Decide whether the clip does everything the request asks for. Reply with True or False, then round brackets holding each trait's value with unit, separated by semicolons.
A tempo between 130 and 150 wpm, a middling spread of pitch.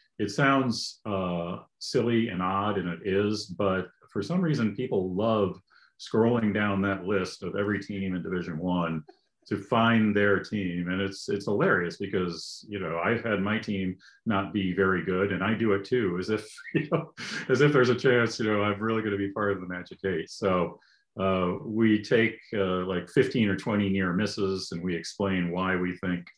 False (200 wpm; 3.0 semitones)